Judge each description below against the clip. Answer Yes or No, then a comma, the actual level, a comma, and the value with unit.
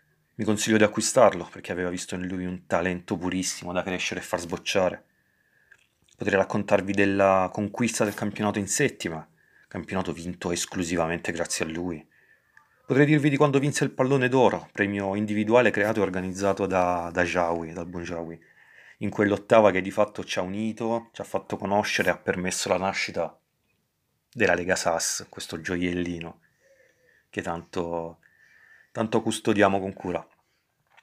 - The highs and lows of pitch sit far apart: No, average, 3.2 semitones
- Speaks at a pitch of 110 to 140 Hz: No, very low, 95 Hz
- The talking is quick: No, average, 150 wpm